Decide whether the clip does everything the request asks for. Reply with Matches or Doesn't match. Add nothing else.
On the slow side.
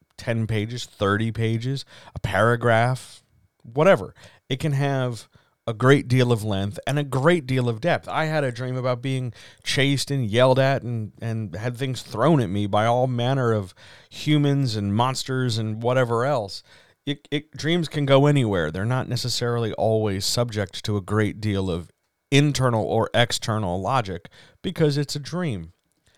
Doesn't match